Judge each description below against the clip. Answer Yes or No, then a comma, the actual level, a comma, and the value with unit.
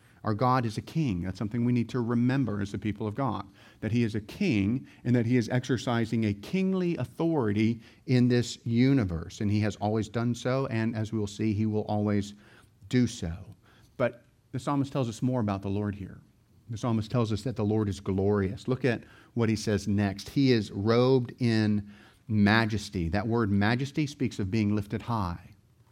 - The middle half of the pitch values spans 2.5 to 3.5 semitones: Yes, average, 3.0 semitones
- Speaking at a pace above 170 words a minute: Yes, average, 195 wpm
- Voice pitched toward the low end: Yes, low, 115 Hz